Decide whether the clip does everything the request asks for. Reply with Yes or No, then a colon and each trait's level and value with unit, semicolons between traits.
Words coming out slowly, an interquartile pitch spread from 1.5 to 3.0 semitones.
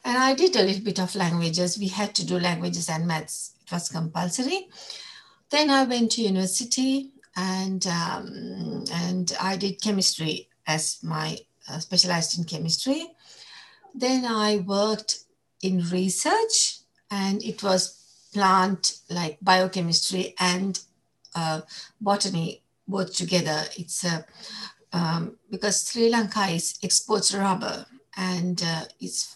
No: slow, 130 wpm; average, 3.5 semitones